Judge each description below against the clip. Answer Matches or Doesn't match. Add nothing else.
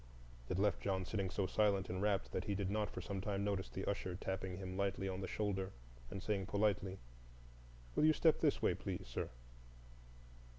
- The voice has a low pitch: Matches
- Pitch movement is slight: Matches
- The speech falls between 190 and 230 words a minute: Matches